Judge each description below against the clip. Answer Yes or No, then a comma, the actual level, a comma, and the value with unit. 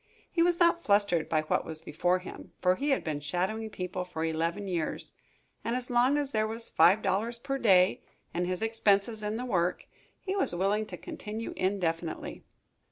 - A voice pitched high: Yes, high, 200 Hz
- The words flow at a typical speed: Yes, average, 185 wpm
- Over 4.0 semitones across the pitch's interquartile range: Yes, average, 4.6 semitones